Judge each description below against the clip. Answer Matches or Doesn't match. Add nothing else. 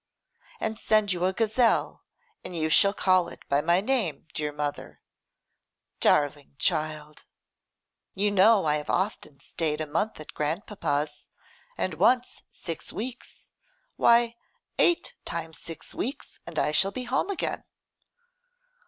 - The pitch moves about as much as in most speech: Doesn't match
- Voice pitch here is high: Doesn't match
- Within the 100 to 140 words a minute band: Matches